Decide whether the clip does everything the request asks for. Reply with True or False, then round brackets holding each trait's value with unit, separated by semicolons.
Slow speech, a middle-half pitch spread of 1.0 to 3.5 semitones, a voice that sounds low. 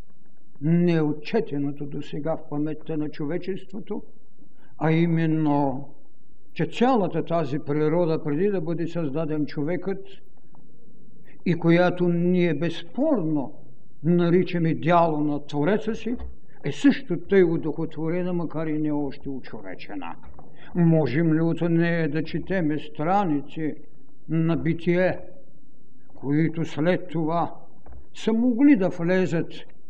False (105 wpm; 2.8 semitones; 165 Hz)